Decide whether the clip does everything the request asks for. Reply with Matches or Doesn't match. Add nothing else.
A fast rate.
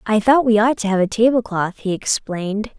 Matches